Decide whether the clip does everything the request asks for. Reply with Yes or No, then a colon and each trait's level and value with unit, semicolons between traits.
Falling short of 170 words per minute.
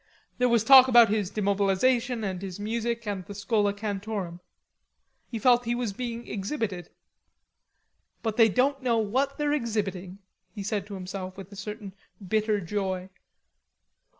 Yes: average, 150 wpm